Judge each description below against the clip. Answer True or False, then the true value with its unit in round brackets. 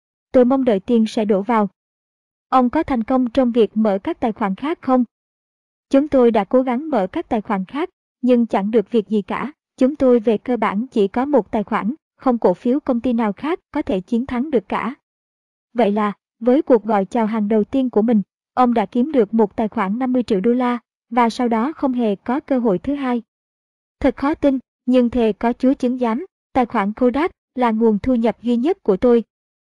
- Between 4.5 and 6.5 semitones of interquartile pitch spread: False (2.7 semitones)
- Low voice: False (240 Hz)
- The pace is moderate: True (225 wpm)